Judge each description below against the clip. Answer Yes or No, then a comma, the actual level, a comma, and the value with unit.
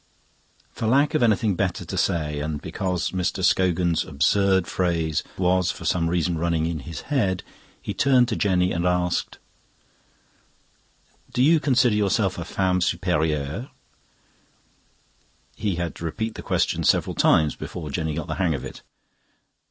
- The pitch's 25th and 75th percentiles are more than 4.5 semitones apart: No, average, 3.6 semitones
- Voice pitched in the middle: No, very low, 90 Hz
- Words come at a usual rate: Yes, average, 150 wpm